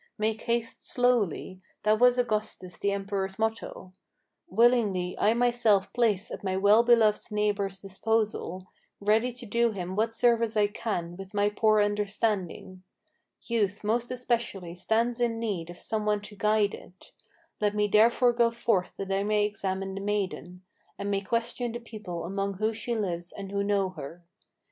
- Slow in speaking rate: No, average, 165 wpm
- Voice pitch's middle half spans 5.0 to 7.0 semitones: No, average, 2.8 semitones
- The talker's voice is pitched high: Yes, high, 210 Hz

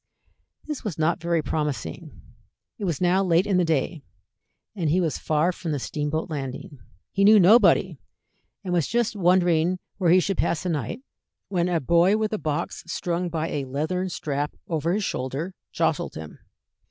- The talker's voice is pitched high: No, medium, 170 Hz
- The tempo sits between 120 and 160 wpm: No, average, 175 wpm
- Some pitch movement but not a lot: Yes, average, 3.4 semitones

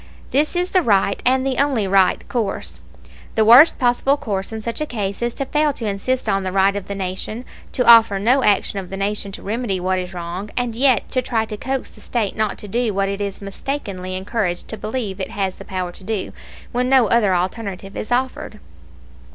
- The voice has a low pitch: No, high, 215 Hz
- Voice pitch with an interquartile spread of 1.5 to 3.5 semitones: No, average, 4.2 semitones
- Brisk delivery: Yes, fast, 215 wpm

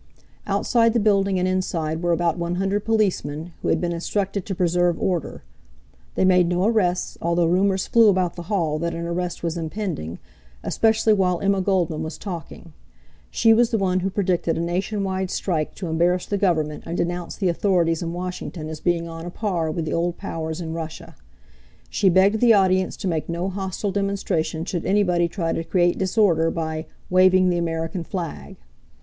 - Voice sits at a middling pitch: Yes, medium, 180 Hz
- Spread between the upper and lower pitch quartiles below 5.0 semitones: Yes, narrow, 2.6 semitones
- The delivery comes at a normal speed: Yes, average, 180 wpm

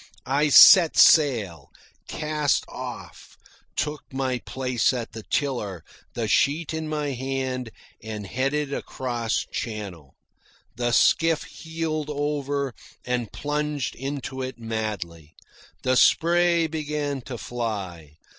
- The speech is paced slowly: Yes, slow, 110 wpm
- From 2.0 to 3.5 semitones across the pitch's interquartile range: No, average, 4.7 semitones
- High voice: No, low, 130 Hz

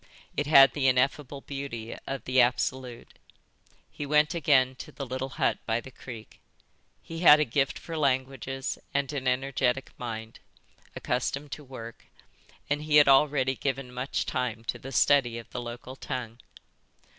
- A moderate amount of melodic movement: No, narrow, 2.2 semitones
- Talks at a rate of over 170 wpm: No, average, 155 wpm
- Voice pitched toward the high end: No, low, 135 Hz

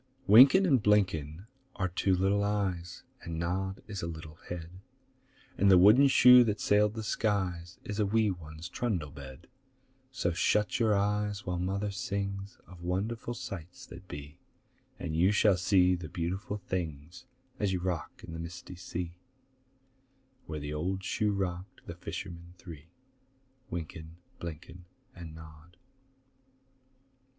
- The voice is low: Yes, very low, 90 Hz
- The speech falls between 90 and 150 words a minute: Yes, average, 140 wpm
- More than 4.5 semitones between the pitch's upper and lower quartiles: No, average, 3.3 semitones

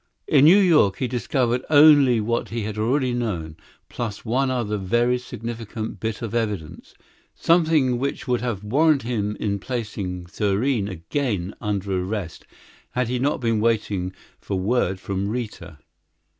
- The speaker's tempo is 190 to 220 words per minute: No, average, 145 wpm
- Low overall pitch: Yes, low, 115 Hz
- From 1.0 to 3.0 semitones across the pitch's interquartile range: No, average, 4.0 semitones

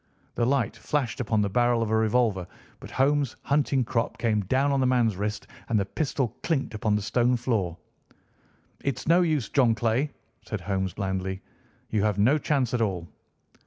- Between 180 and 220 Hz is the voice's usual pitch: No, low, 115 Hz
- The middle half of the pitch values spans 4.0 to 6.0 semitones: Yes, average, 4.3 semitones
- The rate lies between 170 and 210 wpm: Yes, average, 180 wpm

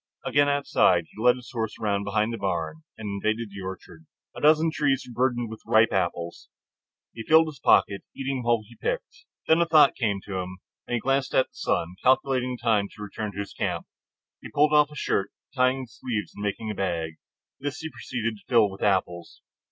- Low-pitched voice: Yes, low, 115 Hz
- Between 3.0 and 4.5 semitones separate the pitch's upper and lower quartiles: No, average, 5.2 semitones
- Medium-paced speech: No, fast, 210 wpm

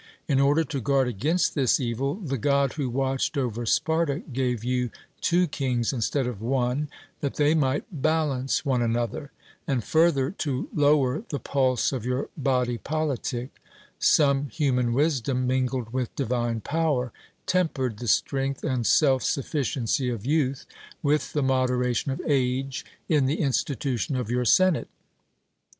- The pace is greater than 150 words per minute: No, average, 145 wpm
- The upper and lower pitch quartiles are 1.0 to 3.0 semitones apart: Yes, narrow, 2.6 semitones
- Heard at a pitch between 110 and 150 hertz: Yes, low, 135 Hz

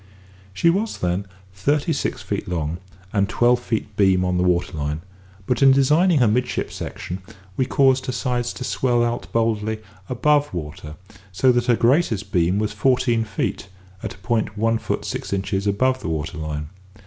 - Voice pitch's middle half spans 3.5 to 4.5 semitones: No, wide, 5.4 semitones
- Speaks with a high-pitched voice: No, low, 110 Hz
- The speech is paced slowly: No, average, 175 wpm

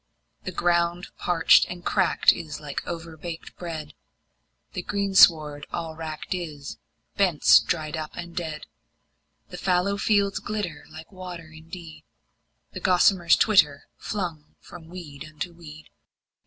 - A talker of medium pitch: Yes, medium, 170 Hz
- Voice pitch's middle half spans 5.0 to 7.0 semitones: No, narrow, 2.6 semitones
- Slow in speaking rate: Yes, slow, 125 wpm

